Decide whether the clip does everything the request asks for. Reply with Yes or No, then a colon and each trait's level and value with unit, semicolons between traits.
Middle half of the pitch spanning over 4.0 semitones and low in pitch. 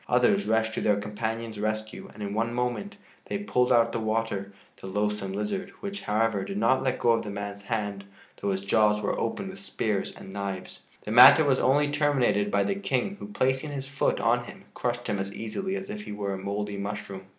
Yes: average, 4.5 semitones; low, 110 Hz